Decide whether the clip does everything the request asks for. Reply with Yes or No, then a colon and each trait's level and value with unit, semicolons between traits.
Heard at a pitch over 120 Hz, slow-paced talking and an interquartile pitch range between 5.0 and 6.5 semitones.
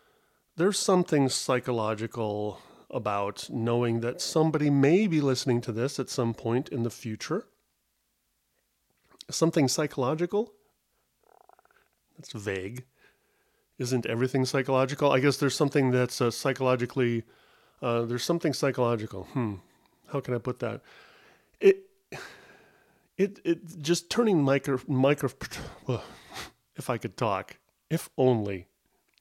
Yes: low, 135 Hz; slow, 115 wpm; wide, 5.4 semitones